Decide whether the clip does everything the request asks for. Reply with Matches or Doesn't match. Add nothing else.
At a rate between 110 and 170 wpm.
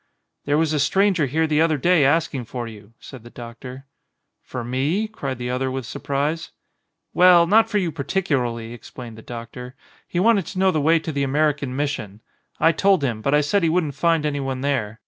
Doesn't match